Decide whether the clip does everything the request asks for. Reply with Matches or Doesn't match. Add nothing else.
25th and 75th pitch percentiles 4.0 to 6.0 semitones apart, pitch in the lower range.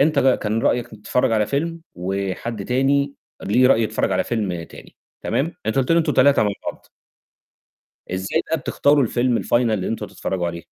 Matches